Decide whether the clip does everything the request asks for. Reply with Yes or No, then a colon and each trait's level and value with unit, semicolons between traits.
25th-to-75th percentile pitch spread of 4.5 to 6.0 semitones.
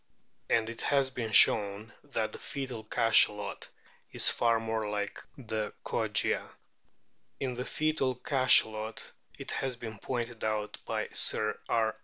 No: average, 2.8 semitones